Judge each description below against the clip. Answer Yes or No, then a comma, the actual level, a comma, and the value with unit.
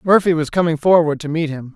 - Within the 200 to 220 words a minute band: No, fast, 240 wpm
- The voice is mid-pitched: Yes, medium, 160 Hz